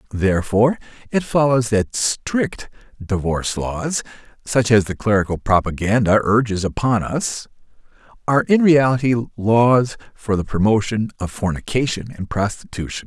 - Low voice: Yes, low, 110 Hz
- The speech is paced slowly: Yes, slow, 120 wpm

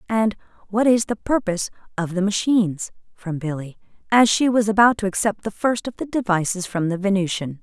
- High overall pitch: Yes, high, 200 Hz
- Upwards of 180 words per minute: Yes, average, 190 wpm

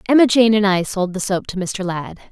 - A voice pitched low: No, high, 200 Hz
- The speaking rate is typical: No, fast, 260 wpm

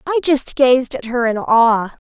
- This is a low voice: No, very high, 250 Hz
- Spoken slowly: No, average, 200 wpm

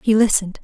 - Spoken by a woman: Yes, female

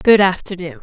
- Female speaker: Yes, female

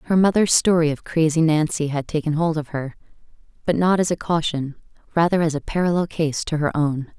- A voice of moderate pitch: Yes, medium, 160 Hz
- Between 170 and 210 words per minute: Yes, average, 200 wpm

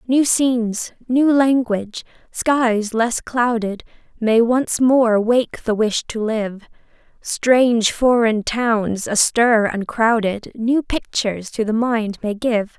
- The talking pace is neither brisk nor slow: No, slow, 130 wpm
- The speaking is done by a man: No, female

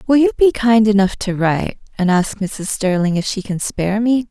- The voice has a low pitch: No, high, 205 Hz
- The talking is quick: Yes, fast, 225 wpm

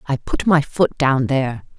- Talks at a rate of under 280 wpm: Yes, average, 200 wpm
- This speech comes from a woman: Yes, female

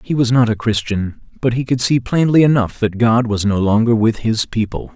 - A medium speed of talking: No, fast, 230 wpm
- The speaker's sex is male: Yes, male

